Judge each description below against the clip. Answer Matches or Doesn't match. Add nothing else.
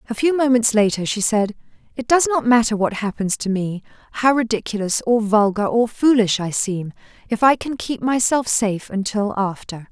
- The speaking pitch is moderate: Doesn't match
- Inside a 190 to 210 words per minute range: Doesn't match